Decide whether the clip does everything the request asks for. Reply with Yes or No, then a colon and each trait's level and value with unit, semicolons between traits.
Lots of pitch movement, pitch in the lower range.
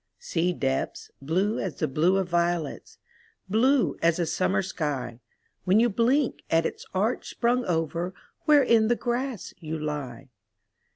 No: wide, 6.3 semitones; medium, 180 Hz